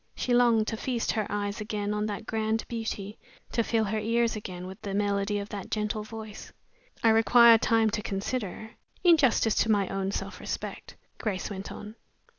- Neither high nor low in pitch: No, high, 215 Hz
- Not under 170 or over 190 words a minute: Yes, average, 185 wpm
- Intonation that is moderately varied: No, narrow, 1.8 semitones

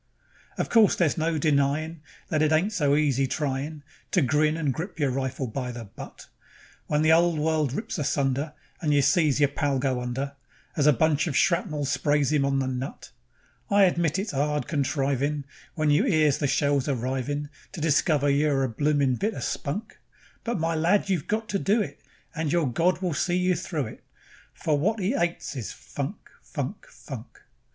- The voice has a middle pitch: Yes, medium, 150 Hz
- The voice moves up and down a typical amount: Yes, average, 3.2 semitones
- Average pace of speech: Yes, average, 185 wpm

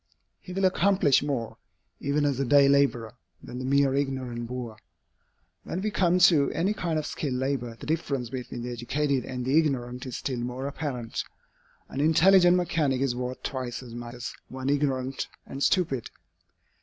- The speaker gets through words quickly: No, average, 170 wpm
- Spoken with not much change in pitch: No, average, 3.3 semitones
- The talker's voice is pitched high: No, low, 135 Hz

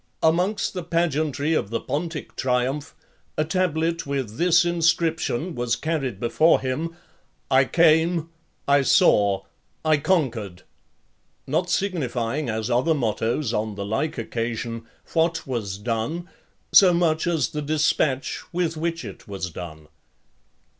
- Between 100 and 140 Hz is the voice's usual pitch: No, medium, 150 Hz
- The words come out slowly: Yes, slow, 125 wpm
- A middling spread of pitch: No, wide, 6.1 semitones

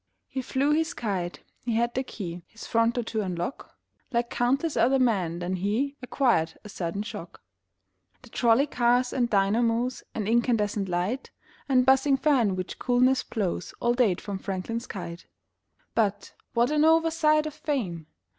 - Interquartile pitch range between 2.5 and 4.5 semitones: No, average, 5.0 semitones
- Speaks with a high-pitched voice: Yes, high, 235 Hz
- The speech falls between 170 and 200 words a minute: No, average, 155 wpm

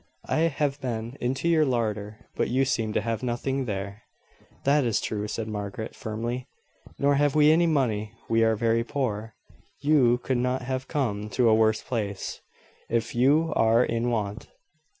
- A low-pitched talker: Yes, low, 120 Hz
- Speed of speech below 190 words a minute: Yes, average, 170 wpm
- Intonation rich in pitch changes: No, average, 3.5 semitones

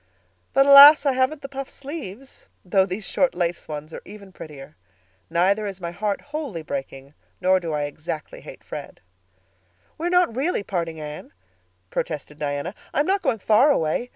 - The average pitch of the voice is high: Yes, high, 195 Hz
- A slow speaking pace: No, average, 165 wpm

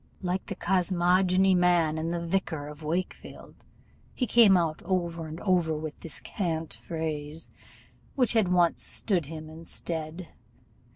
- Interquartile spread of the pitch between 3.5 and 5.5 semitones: No, narrow, 2.5 semitones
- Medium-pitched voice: Yes, medium, 170 Hz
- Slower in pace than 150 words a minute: Yes, average, 140 wpm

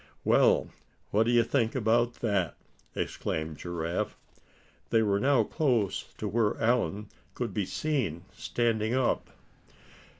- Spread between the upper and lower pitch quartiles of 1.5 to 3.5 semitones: Yes, average, 3.1 semitones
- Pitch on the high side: No, low, 115 Hz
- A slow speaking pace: Yes, slow, 120 wpm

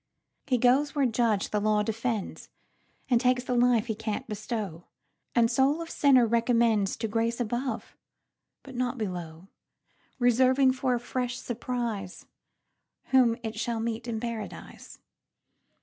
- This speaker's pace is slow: Yes, slow, 120 wpm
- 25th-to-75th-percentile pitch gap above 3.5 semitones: No, narrow, 2.5 semitones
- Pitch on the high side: Yes, high, 235 Hz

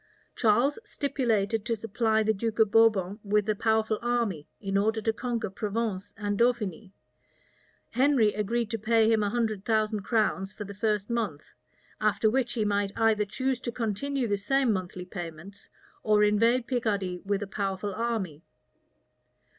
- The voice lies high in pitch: Yes, high, 215 Hz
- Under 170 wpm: Yes, average, 155 wpm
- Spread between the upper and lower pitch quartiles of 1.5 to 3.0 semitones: Yes, narrow, 2.4 semitones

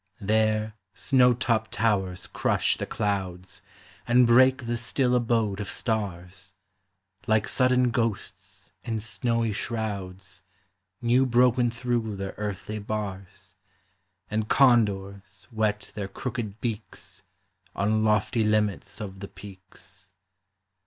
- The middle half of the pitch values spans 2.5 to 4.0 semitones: Yes, average, 3.2 semitones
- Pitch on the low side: Yes, low, 110 Hz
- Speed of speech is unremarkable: No, slow, 110 wpm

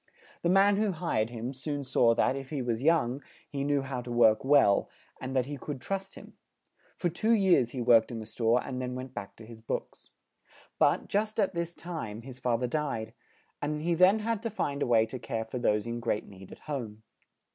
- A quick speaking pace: Yes, fast, 220 wpm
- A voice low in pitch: Yes, low, 130 Hz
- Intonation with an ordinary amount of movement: No, wide, 5.9 semitones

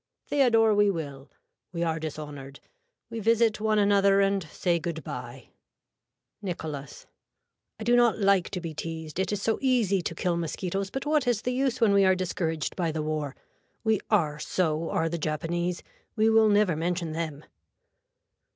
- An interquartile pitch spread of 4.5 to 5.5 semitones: Yes, average, 5.0 semitones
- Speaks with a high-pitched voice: No, medium, 180 Hz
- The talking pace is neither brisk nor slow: Yes, average, 170 wpm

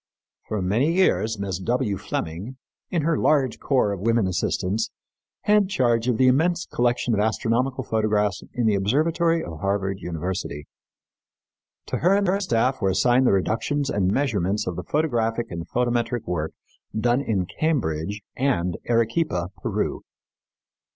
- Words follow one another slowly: No, average, 145 wpm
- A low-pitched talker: Yes, low, 115 Hz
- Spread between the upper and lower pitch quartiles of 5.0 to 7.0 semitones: Yes, wide, 5.5 semitones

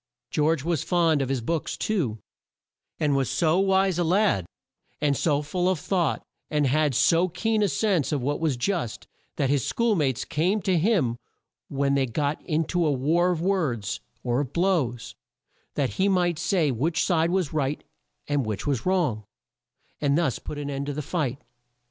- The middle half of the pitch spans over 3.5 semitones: Yes, average, 4.5 semitones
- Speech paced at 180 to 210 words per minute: Yes, average, 185 wpm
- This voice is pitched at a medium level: Yes, medium, 155 Hz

